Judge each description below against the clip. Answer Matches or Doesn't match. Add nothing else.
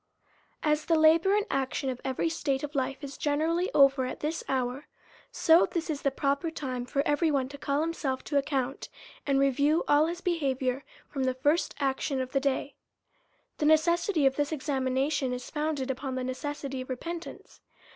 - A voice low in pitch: Doesn't match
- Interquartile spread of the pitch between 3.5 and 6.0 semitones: Doesn't match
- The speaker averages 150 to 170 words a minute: Doesn't match